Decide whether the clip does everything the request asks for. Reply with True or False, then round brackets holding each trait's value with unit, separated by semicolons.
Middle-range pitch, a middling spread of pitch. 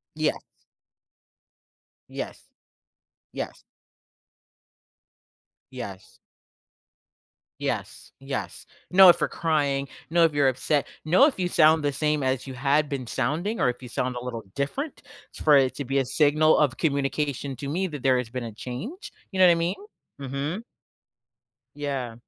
True (145 Hz; 3.6 semitones)